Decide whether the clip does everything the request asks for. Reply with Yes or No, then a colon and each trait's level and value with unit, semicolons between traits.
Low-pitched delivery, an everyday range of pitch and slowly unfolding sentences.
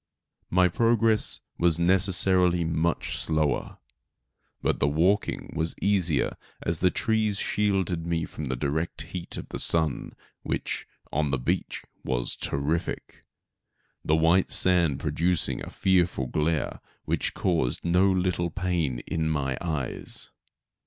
Yes: very low, 85 Hz; average, 3.0 semitones; slow, 125 wpm